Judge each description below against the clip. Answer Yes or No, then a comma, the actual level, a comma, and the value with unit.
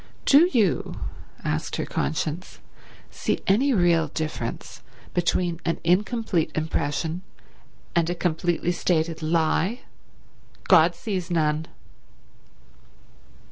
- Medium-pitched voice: Yes, medium, 170 Hz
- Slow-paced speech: Yes, slow, 95 wpm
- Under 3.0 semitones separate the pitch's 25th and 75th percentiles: Yes, narrow, 2.5 semitones